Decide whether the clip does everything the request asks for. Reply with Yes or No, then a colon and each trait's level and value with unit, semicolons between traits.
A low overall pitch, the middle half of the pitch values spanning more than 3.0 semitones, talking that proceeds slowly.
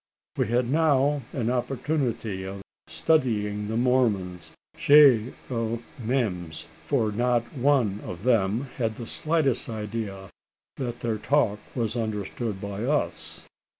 Yes: low, 115 Hz; average, 3.9 semitones; slow, 120 wpm